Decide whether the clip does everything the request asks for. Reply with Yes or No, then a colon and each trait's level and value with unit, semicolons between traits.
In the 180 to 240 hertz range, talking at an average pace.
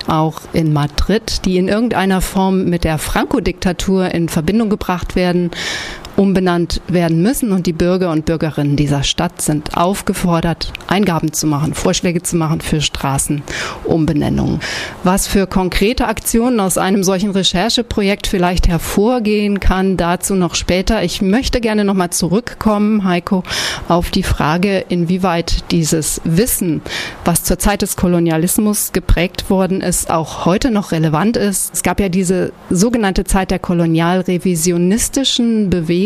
Yes: medium, 185 Hz; average, 135 wpm